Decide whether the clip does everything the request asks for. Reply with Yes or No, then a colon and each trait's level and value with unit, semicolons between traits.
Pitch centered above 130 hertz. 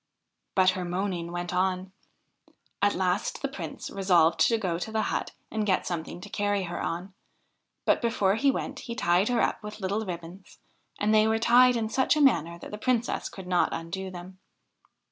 Yes: high, 190 Hz